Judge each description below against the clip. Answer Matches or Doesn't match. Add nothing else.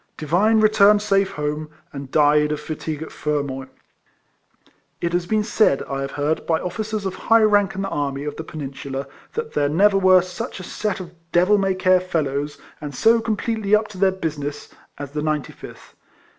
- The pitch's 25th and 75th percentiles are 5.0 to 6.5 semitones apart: Matches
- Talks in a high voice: Doesn't match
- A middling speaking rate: Matches